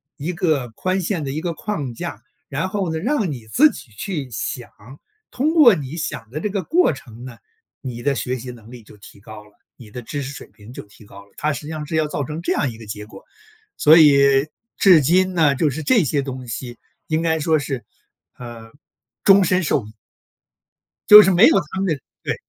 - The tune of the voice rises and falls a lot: Yes, wide, 6.1 semitones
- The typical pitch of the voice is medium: Yes, medium, 145 Hz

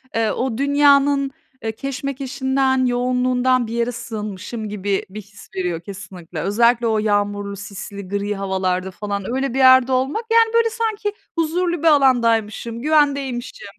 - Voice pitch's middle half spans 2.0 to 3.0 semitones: No, average, 5.1 semitones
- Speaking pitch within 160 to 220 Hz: No, high, 240 Hz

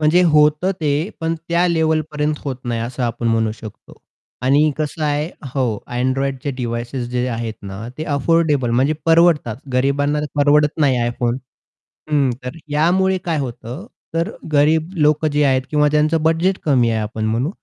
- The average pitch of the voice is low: No, medium, 145 Hz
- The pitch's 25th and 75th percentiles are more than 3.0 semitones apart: Yes, average, 4.2 semitones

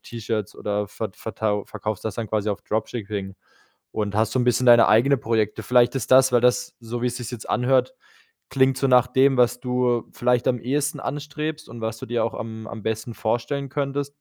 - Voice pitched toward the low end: Yes, low, 120 Hz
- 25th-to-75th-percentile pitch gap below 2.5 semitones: No, average, 2.9 semitones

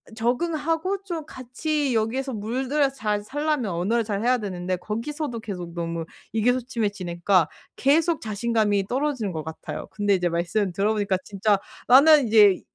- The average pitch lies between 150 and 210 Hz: No, high, 220 Hz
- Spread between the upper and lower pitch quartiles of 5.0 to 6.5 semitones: Yes, wide, 5.4 semitones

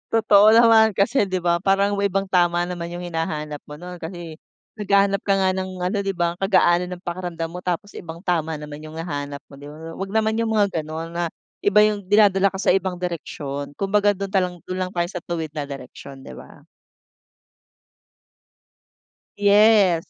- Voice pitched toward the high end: No, medium, 180 Hz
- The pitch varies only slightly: No, average, 3.2 semitones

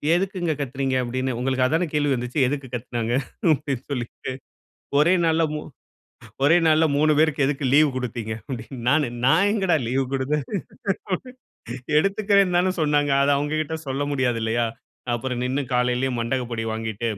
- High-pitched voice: No, low, 135 Hz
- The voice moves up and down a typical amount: Yes, average, 3.8 semitones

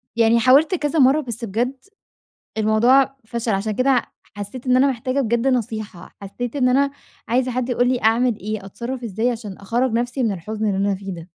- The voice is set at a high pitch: Yes, high, 235 Hz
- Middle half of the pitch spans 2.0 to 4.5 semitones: Yes, average, 3.0 semitones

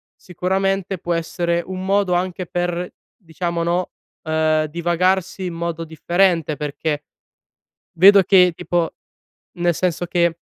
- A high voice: No, medium, 175 Hz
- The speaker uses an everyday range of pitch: No, narrow, 1.7 semitones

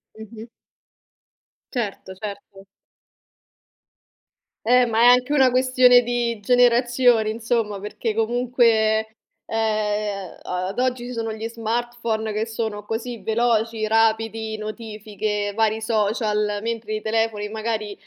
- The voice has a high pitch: Yes, high, 225 Hz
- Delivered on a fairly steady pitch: Yes, narrow, 1.9 semitones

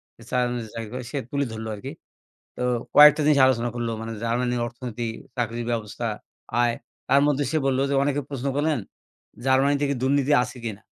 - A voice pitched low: Yes, low, 125 Hz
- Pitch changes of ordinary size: Yes, average, 3.2 semitones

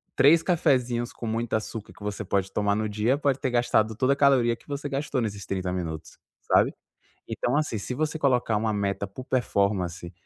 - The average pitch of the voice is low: Yes, low, 115 Hz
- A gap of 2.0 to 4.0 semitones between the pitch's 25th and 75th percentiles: No, average, 4.7 semitones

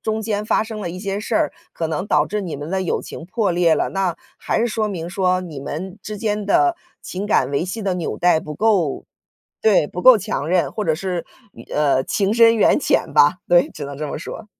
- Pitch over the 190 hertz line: No, medium, 185 Hz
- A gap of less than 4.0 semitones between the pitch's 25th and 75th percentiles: No, average, 4.3 semitones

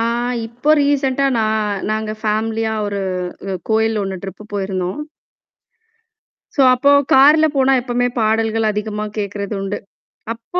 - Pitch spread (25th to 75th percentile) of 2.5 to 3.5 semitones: Yes, average, 3.1 semitones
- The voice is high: Yes, high, 220 Hz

